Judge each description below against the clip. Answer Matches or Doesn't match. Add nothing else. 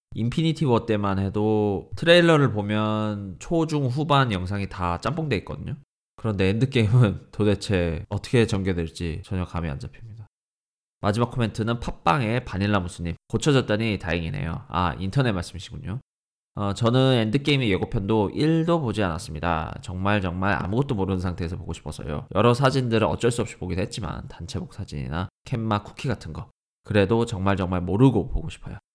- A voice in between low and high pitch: Doesn't match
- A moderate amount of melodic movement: Matches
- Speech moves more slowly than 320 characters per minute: Doesn't match